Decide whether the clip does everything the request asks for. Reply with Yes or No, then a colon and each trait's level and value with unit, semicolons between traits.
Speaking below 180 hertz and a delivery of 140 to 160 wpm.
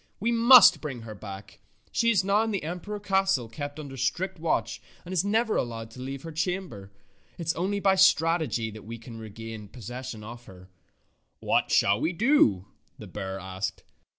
No: medium, 140 Hz; average, 185 wpm